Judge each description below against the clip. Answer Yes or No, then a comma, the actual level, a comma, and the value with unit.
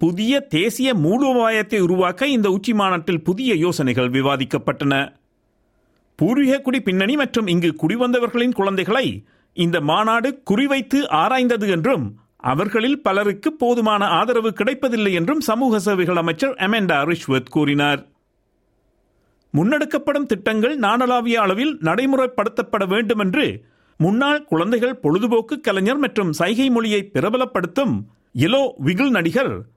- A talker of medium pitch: No, high, 215 Hz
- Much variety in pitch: Yes, wide, 6.8 semitones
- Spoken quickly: No, average, 105 wpm